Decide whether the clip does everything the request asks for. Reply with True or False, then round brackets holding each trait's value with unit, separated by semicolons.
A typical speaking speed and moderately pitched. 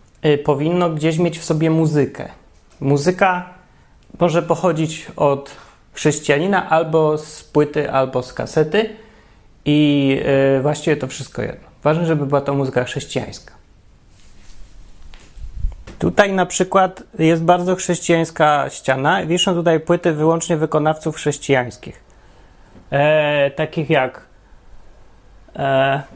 False (105 wpm; 155 Hz)